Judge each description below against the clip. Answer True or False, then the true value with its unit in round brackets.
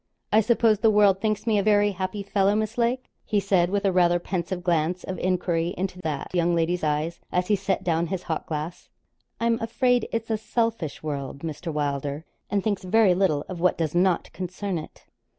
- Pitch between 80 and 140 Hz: False (185 Hz)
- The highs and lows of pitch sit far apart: False (3.7 semitones)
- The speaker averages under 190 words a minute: False (200 wpm)